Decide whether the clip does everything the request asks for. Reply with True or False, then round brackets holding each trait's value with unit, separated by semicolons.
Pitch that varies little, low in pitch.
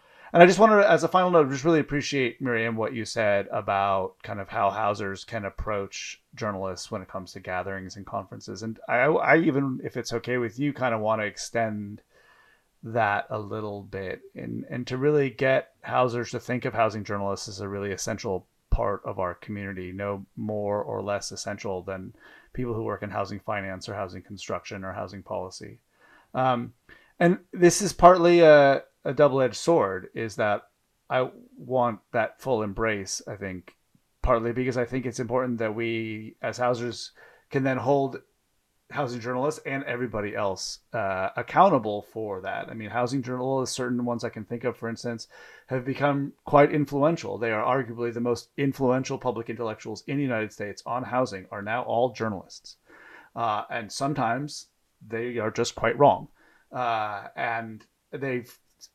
False (4.1 semitones; 115 Hz)